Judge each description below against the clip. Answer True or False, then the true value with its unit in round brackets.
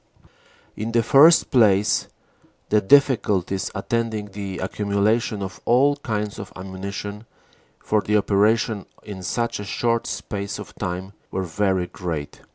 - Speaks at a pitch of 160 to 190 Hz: False (105 Hz)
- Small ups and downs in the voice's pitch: False (3.0 semitones)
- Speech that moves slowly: True (130 wpm)